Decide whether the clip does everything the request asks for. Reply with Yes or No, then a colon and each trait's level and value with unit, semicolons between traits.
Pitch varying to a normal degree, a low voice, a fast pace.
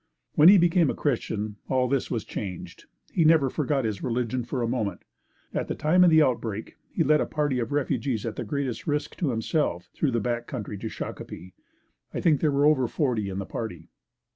Yes: average, 5.0 semitones; low, 130 Hz; fast, 210 wpm